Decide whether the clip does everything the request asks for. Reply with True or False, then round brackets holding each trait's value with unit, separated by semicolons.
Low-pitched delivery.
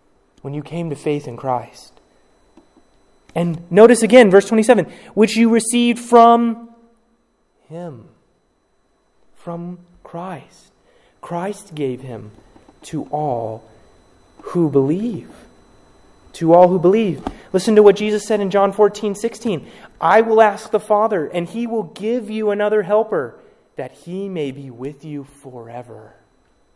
False (180 Hz)